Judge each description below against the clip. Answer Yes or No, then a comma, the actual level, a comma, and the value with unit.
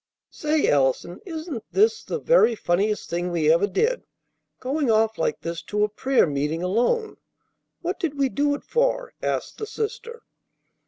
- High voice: Yes, very high, 255 Hz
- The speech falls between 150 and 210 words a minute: Yes, average, 160 wpm